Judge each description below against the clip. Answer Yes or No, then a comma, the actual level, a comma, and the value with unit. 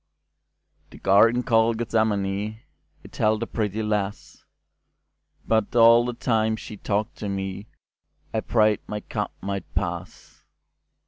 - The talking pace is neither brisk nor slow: No, slow, 110 wpm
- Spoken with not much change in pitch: Yes, narrow, 1.9 semitones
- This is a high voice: No, low, 110 Hz